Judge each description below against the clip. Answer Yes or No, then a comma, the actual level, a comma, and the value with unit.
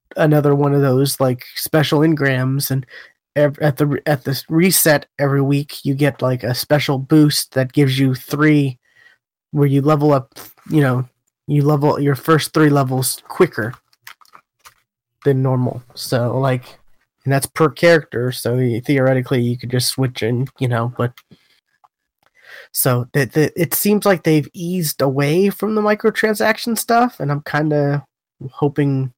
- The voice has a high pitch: No, medium, 140 Hz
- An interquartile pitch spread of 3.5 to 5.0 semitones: No, average, 2.8 semitones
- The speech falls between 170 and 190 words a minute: No, average, 150 wpm